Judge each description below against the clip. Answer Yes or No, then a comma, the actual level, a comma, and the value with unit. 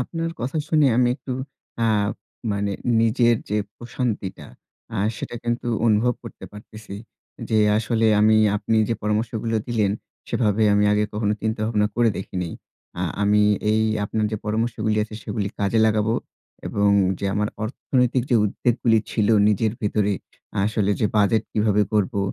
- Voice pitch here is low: Yes, low, 110 Hz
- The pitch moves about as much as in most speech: No, narrow, 1.9 semitones